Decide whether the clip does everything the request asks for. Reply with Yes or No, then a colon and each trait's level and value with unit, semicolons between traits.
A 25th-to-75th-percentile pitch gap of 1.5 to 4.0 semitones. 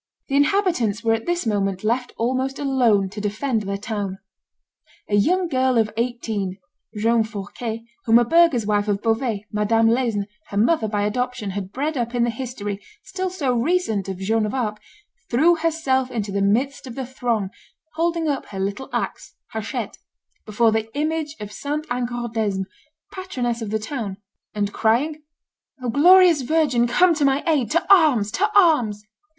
No: average, 5.1 semitones